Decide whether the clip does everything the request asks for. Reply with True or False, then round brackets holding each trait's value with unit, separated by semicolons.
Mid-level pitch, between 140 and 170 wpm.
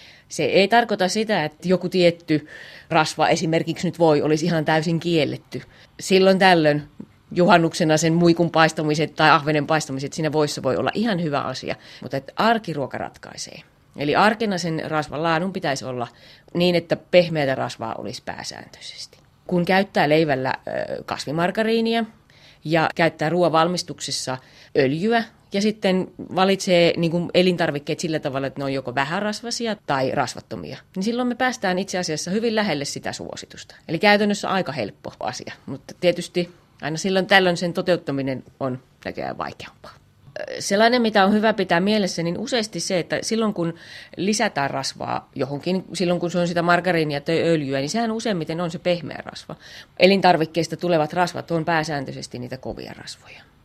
True (170 Hz; 150 wpm)